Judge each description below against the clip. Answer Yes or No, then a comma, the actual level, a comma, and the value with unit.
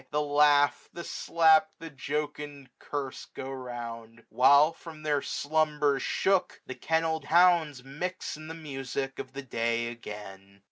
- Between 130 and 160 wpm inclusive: Yes, average, 140 wpm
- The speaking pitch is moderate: Yes, medium, 145 Hz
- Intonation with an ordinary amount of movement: Yes, average, 3.4 semitones